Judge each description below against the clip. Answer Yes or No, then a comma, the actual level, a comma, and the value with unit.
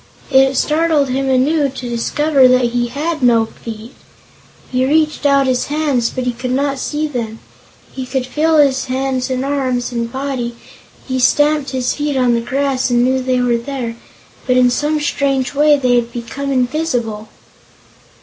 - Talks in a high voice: Yes, very high, 260 Hz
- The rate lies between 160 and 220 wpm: Yes, average, 170 wpm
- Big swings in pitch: No, narrow, 2.4 semitones